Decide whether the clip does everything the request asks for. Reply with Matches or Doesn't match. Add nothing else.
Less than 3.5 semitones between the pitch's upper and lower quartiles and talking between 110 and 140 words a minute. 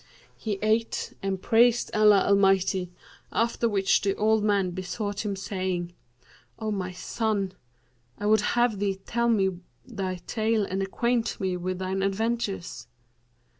Matches